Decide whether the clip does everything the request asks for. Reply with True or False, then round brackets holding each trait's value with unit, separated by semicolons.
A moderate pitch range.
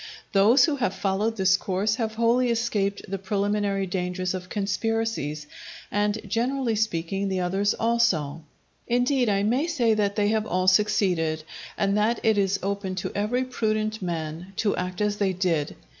True (3.2 semitones)